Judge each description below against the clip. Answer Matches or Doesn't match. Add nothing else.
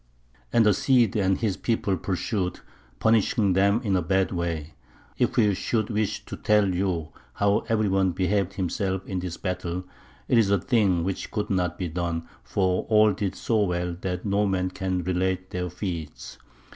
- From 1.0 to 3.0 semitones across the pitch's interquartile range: Matches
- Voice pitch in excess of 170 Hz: Doesn't match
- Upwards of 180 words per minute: Doesn't match